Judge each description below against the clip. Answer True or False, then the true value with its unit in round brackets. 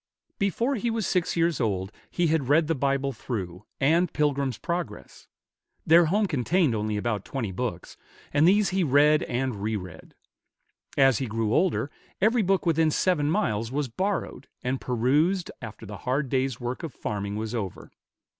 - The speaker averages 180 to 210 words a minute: False (165 wpm)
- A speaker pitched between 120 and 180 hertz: True (135 Hz)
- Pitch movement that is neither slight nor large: False (7.0 semitones)